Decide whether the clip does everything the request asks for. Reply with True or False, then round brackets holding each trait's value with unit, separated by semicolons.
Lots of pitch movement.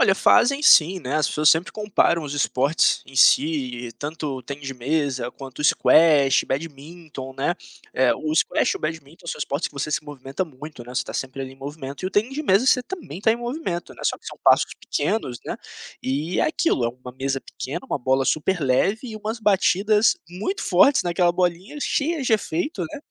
True (6.3 semitones)